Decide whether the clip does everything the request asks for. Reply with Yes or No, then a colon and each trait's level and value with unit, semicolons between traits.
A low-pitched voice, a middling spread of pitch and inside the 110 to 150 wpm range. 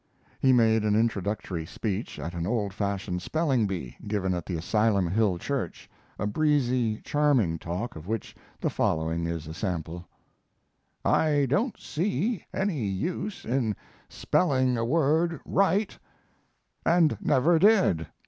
No: low, 110 Hz; wide, 8.3 semitones; slow, 135 wpm